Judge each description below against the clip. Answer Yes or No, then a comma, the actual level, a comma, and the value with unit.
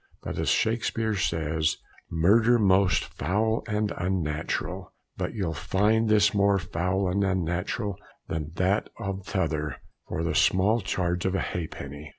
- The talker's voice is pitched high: No, very low, 95 Hz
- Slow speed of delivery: No, average, 145 wpm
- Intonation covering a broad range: No, average, 3.9 semitones